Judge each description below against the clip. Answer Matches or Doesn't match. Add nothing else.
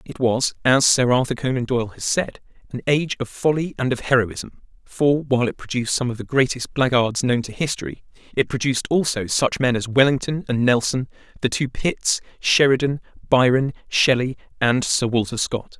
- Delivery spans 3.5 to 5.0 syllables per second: Doesn't match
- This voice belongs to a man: Matches